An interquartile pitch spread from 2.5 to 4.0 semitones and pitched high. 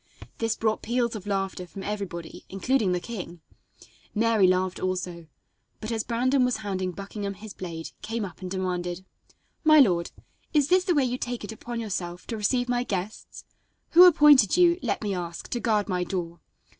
No: average, 4.8 semitones; high, 205 Hz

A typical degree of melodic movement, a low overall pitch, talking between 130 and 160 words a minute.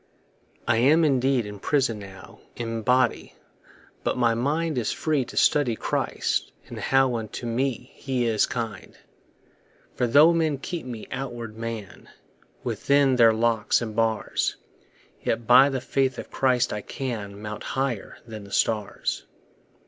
Yes: average, 3.1 semitones; low, 120 Hz; average, 145 wpm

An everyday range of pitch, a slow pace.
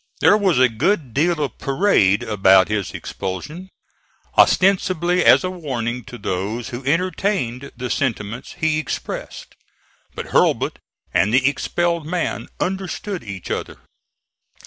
No: wide, 7.7 semitones; slow, 125 wpm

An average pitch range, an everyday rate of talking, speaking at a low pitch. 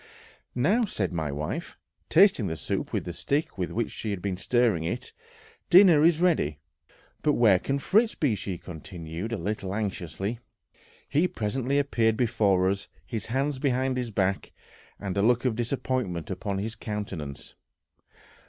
No: wide, 5.8 semitones; average, 155 wpm; low, 110 Hz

